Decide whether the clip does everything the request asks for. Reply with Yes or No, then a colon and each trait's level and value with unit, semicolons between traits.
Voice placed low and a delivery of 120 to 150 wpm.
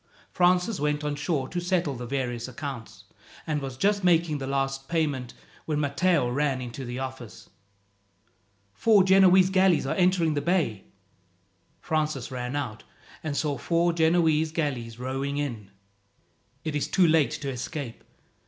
No: medium, 145 Hz; average, 145 wpm